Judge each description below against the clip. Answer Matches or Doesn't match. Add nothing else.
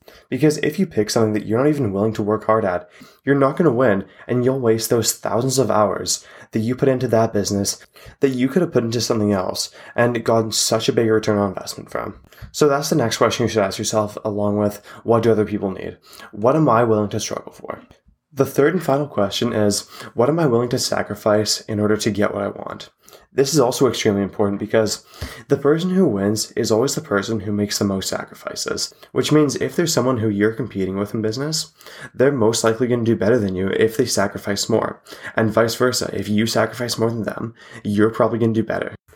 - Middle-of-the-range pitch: Doesn't match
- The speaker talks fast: Matches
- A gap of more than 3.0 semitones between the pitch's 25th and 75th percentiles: Matches